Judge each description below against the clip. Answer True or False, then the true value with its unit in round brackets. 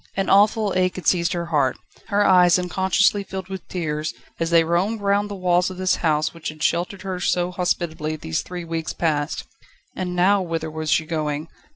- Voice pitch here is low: False (175 Hz)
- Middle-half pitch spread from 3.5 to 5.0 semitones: False (2.8 semitones)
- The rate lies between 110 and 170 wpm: False (195 wpm)